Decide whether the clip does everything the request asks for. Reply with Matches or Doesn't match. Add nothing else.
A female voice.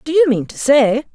Matches